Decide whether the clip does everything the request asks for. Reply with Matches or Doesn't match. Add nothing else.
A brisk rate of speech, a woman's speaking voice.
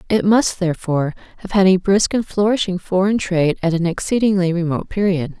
Doesn't match